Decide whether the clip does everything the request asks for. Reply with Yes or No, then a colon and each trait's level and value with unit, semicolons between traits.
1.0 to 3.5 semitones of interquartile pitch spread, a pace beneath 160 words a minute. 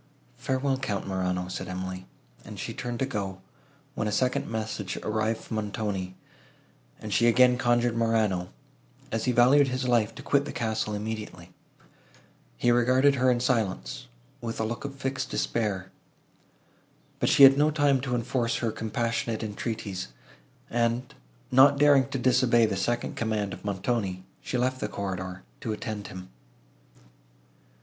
No: average, 3.9 semitones; average, 150 wpm